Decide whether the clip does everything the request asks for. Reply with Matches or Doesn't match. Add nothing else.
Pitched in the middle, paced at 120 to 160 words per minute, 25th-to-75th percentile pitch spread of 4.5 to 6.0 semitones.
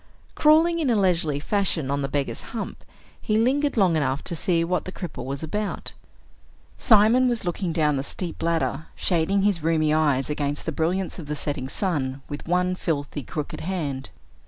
Doesn't match